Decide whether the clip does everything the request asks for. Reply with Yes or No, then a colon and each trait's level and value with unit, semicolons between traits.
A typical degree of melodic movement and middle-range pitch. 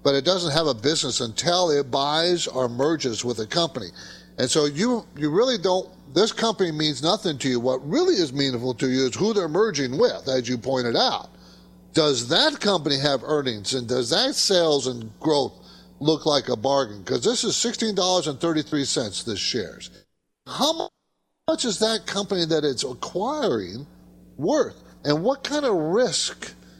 No: wide, 6.2 semitones; medium, 150 Hz